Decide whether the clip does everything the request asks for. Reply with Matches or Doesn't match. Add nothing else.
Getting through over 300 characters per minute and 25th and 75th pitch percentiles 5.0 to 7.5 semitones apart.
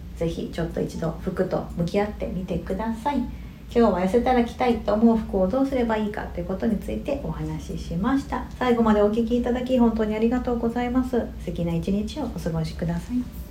Matches